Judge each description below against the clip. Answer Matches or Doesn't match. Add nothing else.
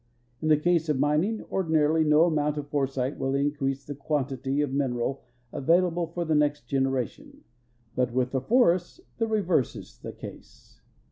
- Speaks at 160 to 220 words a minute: Matches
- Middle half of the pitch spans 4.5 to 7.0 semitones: Doesn't match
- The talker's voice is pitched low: Doesn't match